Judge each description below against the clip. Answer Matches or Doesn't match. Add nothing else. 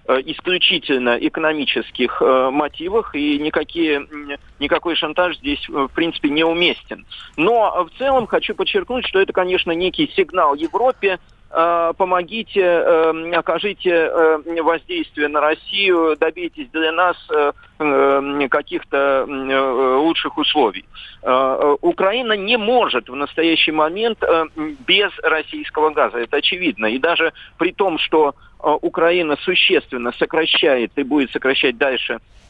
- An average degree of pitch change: Matches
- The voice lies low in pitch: Doesn't match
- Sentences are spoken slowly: Matches